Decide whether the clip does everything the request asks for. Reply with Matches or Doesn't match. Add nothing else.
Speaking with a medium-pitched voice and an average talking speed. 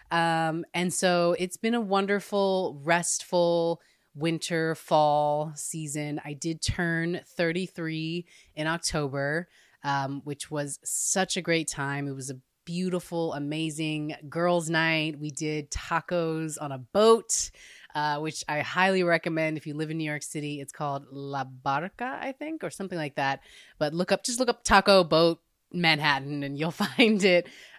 Matches